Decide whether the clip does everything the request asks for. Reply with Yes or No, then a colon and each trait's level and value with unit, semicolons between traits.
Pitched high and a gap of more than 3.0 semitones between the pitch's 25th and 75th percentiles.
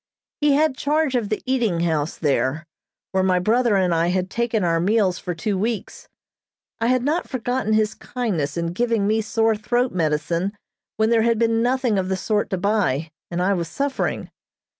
Yes: high, 210 Hz; average, 5.1 semitones